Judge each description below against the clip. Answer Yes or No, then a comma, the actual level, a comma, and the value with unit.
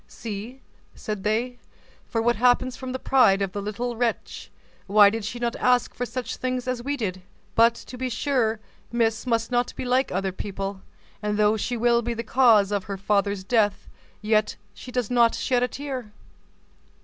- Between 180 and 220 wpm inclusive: Yes, average, 185 wpm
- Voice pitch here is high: Yes, high, 230 Hz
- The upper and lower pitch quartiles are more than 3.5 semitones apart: No, average, 3.1 semitones